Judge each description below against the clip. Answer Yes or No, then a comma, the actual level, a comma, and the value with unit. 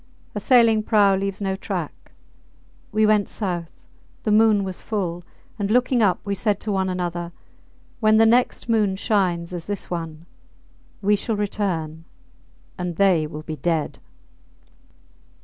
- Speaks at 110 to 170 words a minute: Yes, average, 145 wpm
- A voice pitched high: Yes, high, 195 Hz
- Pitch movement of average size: Yes, average, 3.6 semitones